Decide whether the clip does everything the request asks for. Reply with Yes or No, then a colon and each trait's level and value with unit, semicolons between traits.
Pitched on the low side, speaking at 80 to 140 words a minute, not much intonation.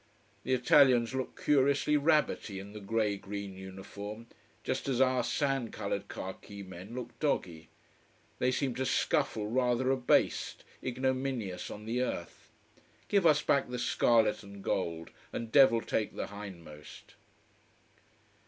No: low, 115 Hz; slow, 135 wpm; average, 4.6 semitones